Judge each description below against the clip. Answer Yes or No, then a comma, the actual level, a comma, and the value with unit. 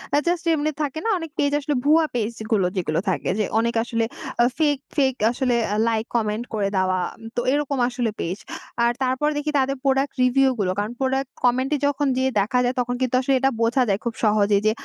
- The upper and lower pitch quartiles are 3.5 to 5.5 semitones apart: Yes, average, 4.1 semitones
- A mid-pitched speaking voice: No, very high, 250 Hz